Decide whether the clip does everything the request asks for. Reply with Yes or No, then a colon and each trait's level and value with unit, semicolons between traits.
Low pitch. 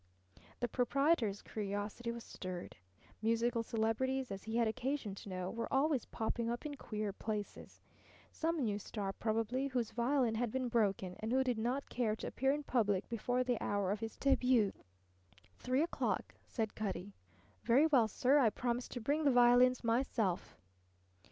No: high, 235 Hz